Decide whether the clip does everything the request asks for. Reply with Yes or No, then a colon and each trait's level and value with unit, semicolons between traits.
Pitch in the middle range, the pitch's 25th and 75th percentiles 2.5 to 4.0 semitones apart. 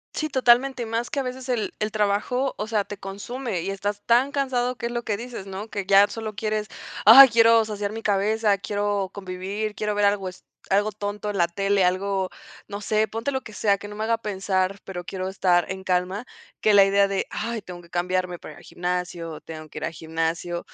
No: high, 205 Hz; average, 2.9 semitones